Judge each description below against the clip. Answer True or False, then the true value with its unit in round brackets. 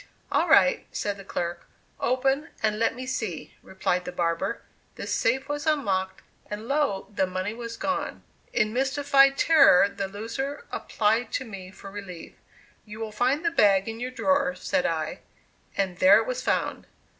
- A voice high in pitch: True (225 Hz)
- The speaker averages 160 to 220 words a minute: True (170 wpm)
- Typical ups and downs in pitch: False (5.8 semitones)